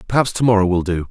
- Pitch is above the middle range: No, low, 105 Hz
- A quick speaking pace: Yes, fast, 270 wpm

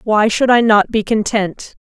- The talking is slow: No, average, 200 wpm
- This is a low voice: No, high, 220 Hz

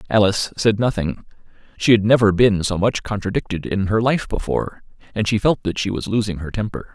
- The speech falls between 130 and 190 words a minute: No, average, 200 wpm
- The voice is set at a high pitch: No, low, 105 Hz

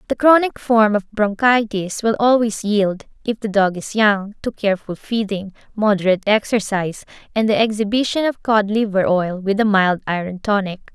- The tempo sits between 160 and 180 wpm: Yes, average, 165 wpm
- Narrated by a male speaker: No, female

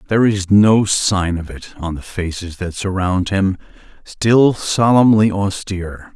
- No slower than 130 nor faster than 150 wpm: Yes, slow, 135 wpm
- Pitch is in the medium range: No, low, 100 Hz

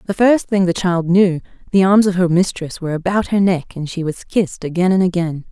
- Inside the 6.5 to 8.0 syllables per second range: No, 5.7 syllables/s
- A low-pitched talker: No, medium, 180 Hz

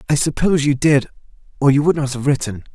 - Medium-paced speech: No, fast, 220 wpm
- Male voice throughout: Yes, male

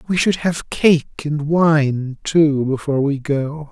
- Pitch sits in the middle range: Yes, medium, 150 Hz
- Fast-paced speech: No, average, 160 wpm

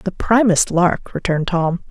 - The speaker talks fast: No, average, 155 wpm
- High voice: No, medium, 180 Hz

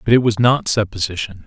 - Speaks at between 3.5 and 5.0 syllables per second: No, 5.8 syllables/s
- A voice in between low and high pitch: No, low, 110 Hz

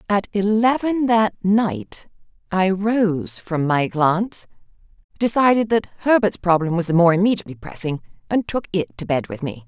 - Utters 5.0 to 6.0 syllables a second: No, 4.8 syllables/s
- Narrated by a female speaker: Yes, female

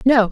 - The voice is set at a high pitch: Yes, high, 230 Hz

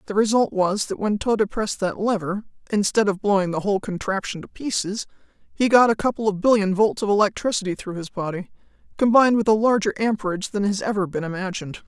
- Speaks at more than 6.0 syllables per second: Yes, 6.2 syllables/s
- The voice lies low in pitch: No, high, 205 Hz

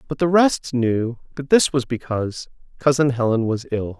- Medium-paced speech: Yes, average, 180 wpm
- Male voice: Yes, male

